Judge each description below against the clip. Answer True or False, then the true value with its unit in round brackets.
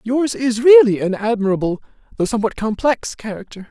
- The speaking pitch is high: True (215 Hz)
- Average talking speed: True (145 wpm)